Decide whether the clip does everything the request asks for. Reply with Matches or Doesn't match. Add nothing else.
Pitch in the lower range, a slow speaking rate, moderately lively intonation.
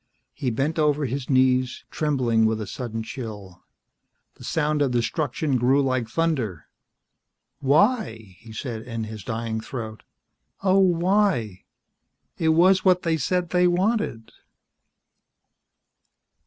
Doesn't match